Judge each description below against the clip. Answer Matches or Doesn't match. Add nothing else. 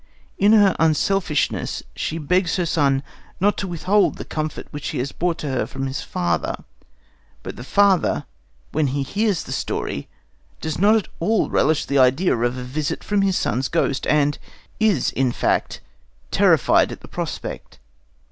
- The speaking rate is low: Doesn't match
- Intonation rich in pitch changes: Matches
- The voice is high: Doesn't match